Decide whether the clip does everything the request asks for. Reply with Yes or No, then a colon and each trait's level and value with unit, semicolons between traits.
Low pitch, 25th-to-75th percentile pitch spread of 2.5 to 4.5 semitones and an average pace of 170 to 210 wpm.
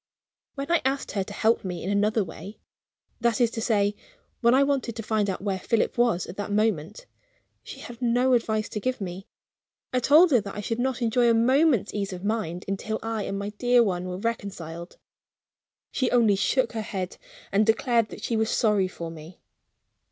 No: high, 220 Hz; average, 3.4 semitones; average, 200 wpm